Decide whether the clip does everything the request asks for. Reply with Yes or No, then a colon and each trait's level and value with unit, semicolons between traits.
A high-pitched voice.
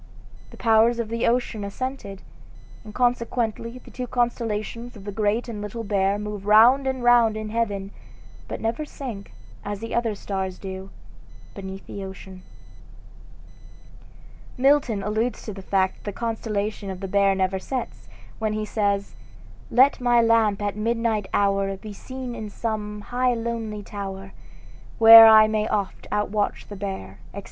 Yes: high, 215 Hz